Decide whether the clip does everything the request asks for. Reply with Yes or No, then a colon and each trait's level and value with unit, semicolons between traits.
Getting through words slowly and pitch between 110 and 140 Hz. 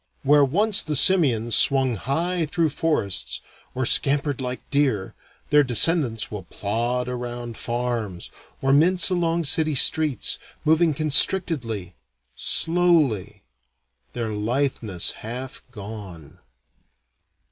Yes: slow, 105 wpm; low, 135 Hz